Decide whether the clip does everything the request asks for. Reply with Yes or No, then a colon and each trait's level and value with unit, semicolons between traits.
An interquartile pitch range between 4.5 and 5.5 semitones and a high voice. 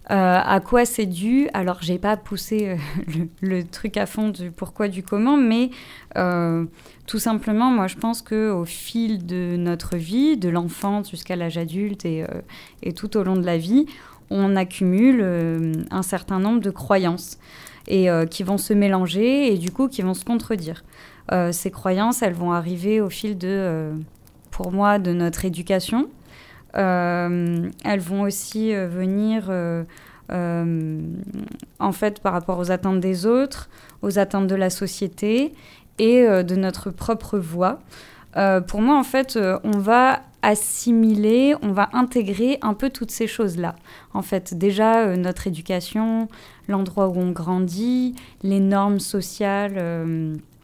No: average, 3.4 semitones; high, 195 Hz